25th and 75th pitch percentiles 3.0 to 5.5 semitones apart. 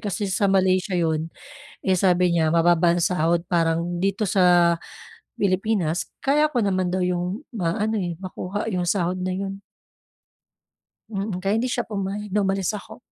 No: narrow, 2.4 semitones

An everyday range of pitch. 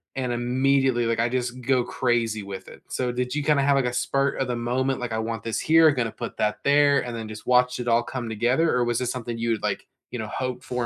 No: narrow, 2.1 semitones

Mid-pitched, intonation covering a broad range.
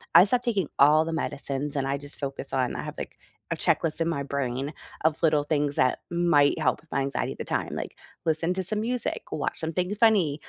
No: medium, 155 Hz; average, 3.6 semitones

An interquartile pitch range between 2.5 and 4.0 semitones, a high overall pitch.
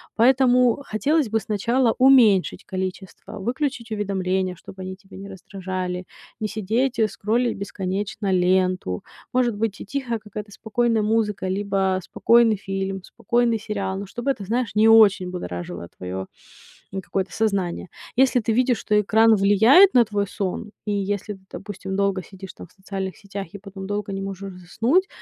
Yes: average, 3.0 semitones; high, 205 Hz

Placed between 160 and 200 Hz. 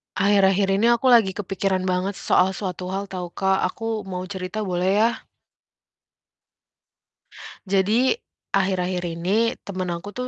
Yes: high, 190 Hz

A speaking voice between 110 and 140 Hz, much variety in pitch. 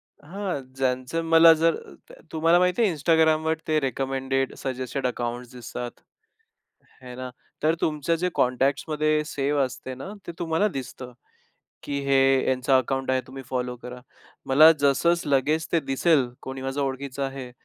No: low, 135 Hz; average, 3.5 semitones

